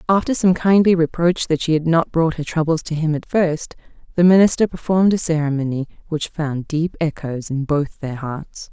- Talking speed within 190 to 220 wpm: Yes, average, 195 wpm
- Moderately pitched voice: Yes, medium, 160 Hz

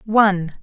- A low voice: No, high, 195 Hz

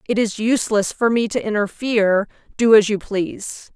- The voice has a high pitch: Yes, high, 215 Hz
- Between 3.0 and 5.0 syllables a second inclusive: No, 5.2 syllables/s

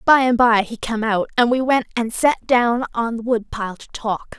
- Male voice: No, female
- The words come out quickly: Yes, fast, 235 wpm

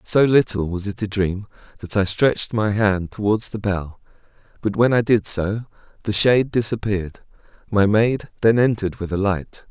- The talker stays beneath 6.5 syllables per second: Yes, 4.9 syllables/s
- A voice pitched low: Yes, low, 105 Hz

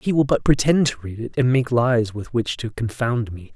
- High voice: No, low, 120 Hz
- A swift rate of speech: Yes, fast, 255 wpm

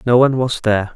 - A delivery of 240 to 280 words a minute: Yes, fast, 250 wpm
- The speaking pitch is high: No, low, 120 Hz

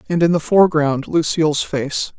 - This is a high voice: No, medium, 155 Hz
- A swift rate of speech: No, average, 165 wpm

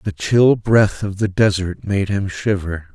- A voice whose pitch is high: No, low, 100 Hz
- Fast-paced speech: No, average, 185 wpm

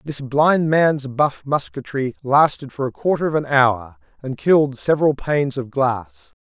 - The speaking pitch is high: No, low, 135 Hz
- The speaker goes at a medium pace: Yes, average, 170 wpm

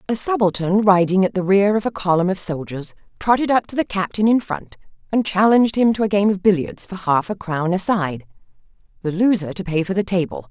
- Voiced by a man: No, female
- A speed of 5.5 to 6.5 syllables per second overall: Yes, 5.7 syllables/s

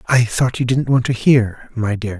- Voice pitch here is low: Yes, low, 120 Hz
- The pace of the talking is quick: Yes, fast, 245 wpm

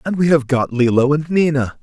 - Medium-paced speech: No, fast, 230 wpm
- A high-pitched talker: No, medium, 145 Hz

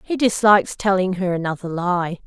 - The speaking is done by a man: No, female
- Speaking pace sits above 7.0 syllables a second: No, 5.2 syllables/s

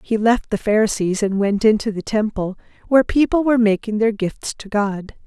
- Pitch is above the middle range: Yes, high, 215 Hz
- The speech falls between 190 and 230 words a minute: Yes, average, 195 wpm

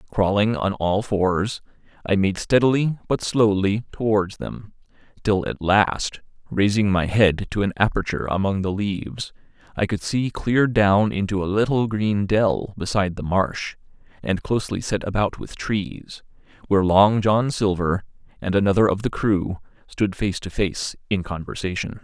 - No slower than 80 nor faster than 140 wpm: No, average, 155 wpm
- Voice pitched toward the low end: Yes, low, 100 Hz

